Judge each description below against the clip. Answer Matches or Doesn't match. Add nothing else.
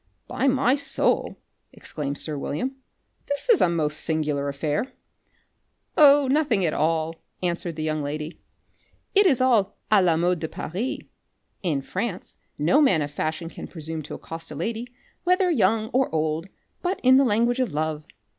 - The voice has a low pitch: Doesn't match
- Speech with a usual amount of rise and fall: Doesn't match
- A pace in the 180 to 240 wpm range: Doesn't match